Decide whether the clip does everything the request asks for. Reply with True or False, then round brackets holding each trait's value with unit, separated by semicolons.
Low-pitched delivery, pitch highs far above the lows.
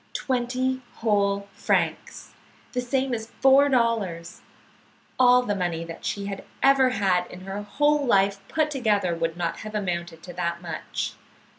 False (205 Hz; 6.0 semitones)